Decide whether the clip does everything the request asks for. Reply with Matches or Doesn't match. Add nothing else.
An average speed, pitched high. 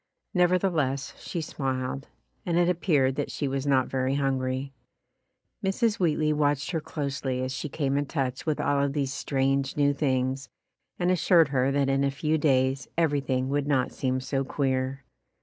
Doesn't match